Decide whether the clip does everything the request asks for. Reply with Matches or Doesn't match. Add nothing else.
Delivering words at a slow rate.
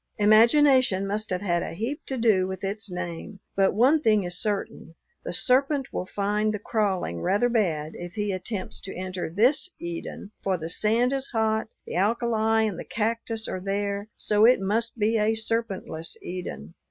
Doesn't match